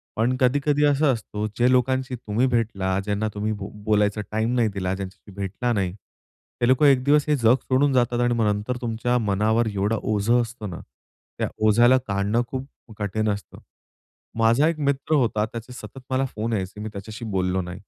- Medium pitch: No, low, 115 Hz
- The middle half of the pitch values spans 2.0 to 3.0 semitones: No, average, 3.6 semitones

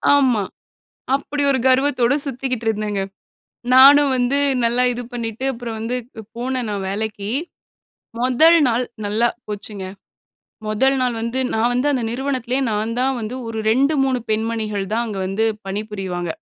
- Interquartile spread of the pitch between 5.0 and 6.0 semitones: No, average, 3.3 semitones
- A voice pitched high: Yes, high, 235 Hz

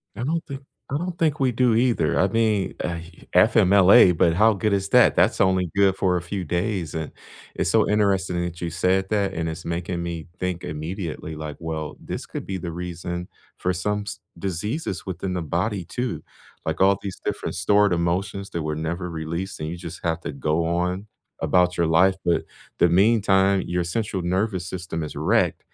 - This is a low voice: Yes, very low, 90 Hz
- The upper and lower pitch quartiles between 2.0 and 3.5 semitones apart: Yes, average, 2.8 semitones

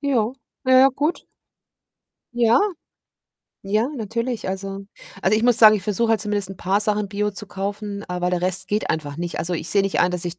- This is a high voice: Yes, high, 205 Hz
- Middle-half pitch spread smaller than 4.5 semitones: Yes, average, 2.9 semitones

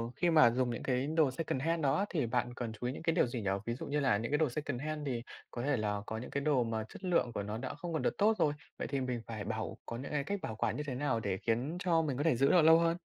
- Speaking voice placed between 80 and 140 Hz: Yes, low, 135 Hz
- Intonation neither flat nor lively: Yes, average, 4.9 semitones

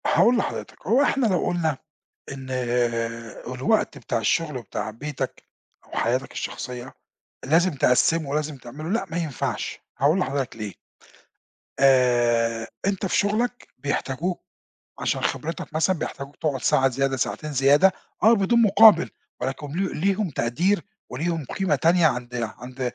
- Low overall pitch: No, medium, 150 Hz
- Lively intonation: Yes, wide, 6.2 semitones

